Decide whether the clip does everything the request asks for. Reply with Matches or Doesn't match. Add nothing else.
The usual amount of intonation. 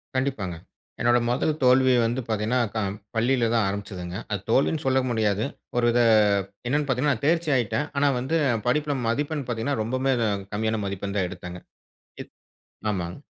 Matches